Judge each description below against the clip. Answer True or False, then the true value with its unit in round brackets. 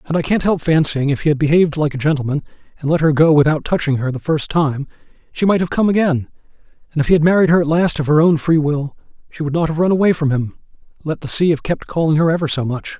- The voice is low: False (155 Hz)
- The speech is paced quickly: True (270 wpm)